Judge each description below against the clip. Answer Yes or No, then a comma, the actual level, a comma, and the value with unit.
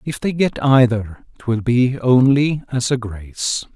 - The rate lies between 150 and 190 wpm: Yes, average, 160 wpm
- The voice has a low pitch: Yes, low, 125 Hz